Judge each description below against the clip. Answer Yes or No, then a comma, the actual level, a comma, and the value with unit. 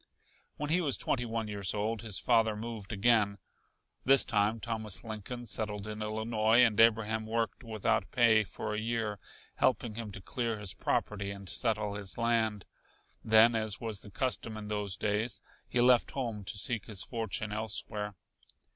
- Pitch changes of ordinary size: No, narrow, 1.9 semitones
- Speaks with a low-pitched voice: Yes, low, 110 Hz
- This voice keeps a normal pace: Yes, average, 165 wpm